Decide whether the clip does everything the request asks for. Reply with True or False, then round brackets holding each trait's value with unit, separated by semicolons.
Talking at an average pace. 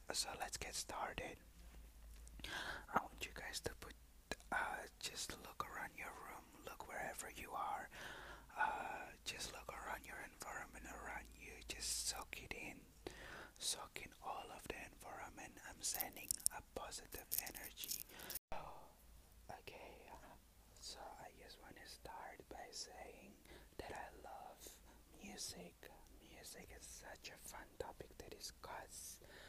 False (130 wpm)